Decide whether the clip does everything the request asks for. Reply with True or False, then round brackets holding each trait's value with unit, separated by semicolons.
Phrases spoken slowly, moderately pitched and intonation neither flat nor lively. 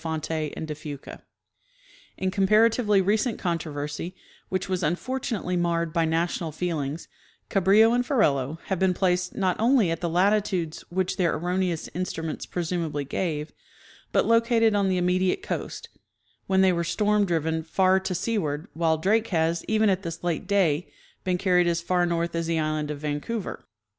False (165 wpm; 180 Hz; 3.3 semitones)